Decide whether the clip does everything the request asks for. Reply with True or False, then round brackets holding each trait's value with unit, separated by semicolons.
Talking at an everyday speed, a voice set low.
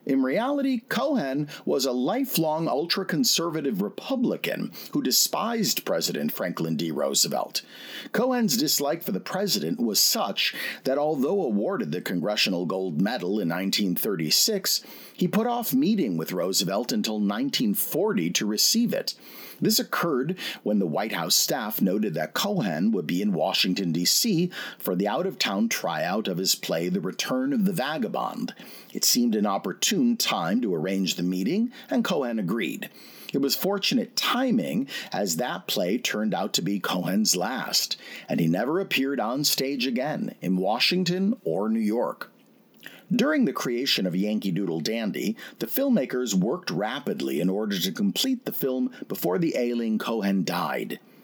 False (150 wpm; 195 Hz)